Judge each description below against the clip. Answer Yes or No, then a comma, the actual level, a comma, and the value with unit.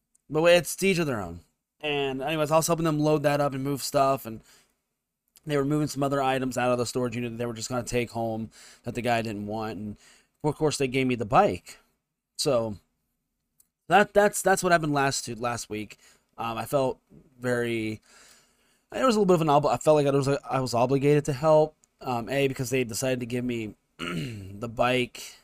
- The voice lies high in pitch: No, low, 130 Hz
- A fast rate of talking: Yes, fast, 215 wpm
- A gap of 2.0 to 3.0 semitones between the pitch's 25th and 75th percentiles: No, average, 3.9 semitones